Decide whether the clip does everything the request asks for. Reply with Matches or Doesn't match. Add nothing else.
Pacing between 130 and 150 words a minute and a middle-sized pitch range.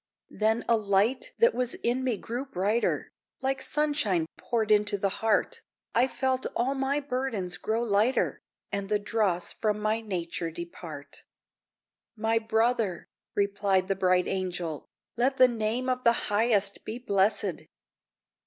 Matches